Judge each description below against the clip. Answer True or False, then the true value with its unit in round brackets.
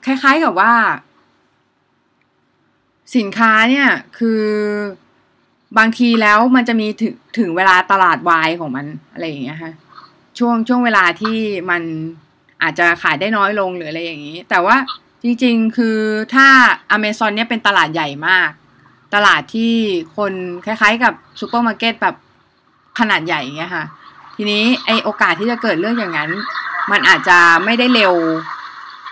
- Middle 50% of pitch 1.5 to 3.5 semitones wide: False (4.8 semitones)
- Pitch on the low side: False (215 Hz)